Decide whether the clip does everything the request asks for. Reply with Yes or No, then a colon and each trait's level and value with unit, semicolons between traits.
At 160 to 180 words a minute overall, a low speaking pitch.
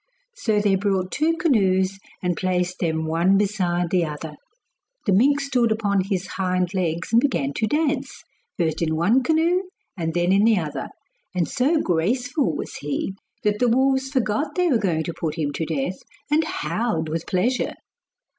No: average, 175 wpm; high, 195 Hz